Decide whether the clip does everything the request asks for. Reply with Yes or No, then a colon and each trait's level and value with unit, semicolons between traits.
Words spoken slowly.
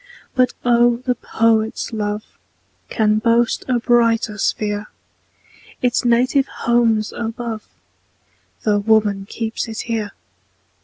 Yes: slow, 105 wpm